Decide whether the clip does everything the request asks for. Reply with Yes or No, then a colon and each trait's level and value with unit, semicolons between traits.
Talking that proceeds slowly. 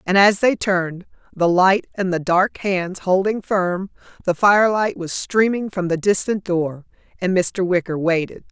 No: average, 170 wpm